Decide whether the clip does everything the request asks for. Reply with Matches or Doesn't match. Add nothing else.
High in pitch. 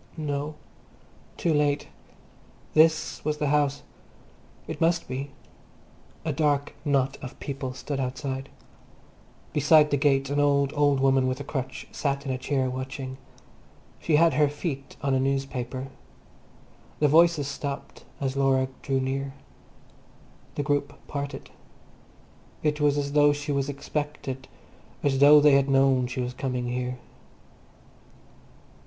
Doesn't match